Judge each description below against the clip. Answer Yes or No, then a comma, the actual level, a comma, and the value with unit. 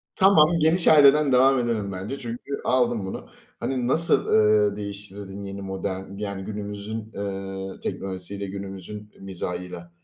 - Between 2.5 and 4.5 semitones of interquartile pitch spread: Yes, average, 4.1 semitones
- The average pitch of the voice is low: Yes, low, 100 Hz